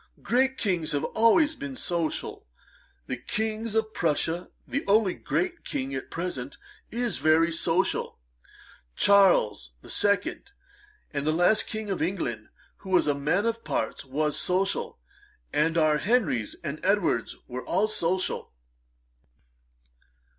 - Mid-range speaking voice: Yes, medium, 180 Hz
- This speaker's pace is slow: Yes, slow, 125 wpm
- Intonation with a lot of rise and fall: Yes, wide, 6.2 semitones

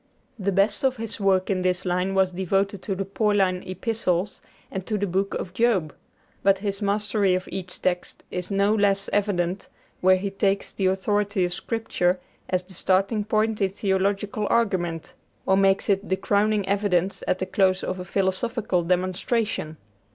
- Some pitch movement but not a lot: No, narrow, 1.9 semitones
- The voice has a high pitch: Yes, high, 195 Hz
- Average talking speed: Yes, average, 170 wpm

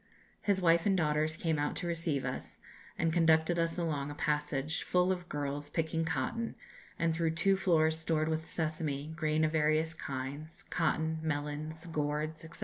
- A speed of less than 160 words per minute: No, average, 165 wpm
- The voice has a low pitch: No, medium, 160 Hz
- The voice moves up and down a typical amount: No, narrow, 1.8 semitones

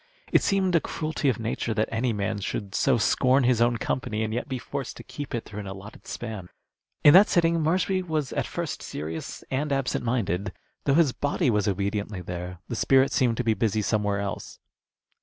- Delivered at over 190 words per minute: Yes, average, 200 wpm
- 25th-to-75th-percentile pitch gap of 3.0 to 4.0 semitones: No, average, 5.1 semitones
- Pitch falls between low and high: No, low, 115 Hz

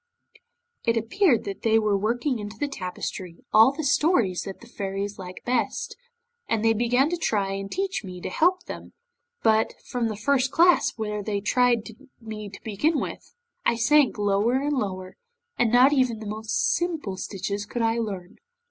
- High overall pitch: Yes, high, 225 Hz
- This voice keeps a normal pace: Yes, average, 175 wpm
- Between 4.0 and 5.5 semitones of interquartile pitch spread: Yes, average, 4.6 semitones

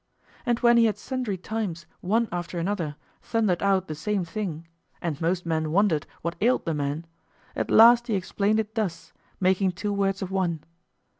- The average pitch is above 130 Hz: Yes, high, 190 Hz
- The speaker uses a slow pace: No, average, 175 wpm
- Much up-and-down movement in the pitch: No, average, 4.2 semitones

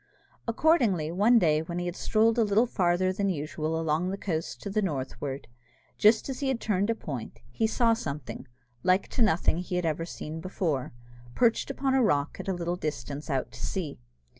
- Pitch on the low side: No, medium, 180 Hz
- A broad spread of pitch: Yes, wide, 5.8 semitones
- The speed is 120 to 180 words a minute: No, average, 190 wpm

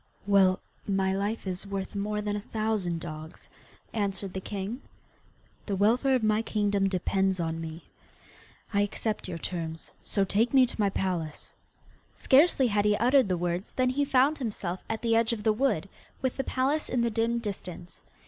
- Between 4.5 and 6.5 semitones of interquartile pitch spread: No, average, 3.6 semitones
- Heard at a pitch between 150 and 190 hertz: No, high, 205 Hz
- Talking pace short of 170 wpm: No, average, 175 wpm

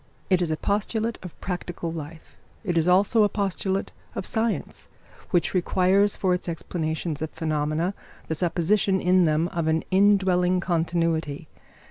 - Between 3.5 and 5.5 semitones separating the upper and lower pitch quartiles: No, average, 2.9 semitones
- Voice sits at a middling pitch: Yes, medium, 180 Hz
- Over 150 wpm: No, average, 145 wpm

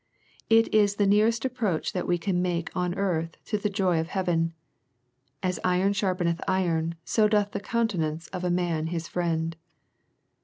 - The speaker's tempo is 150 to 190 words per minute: Yes, average, 175 wpm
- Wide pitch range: No, average, 3.4 semitones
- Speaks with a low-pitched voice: No, medium, 180 Hz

